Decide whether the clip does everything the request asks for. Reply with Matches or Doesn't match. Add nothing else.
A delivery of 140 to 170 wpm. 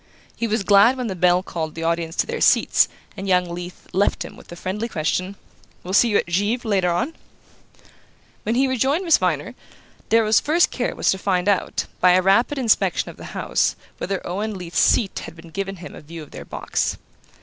Doesn't match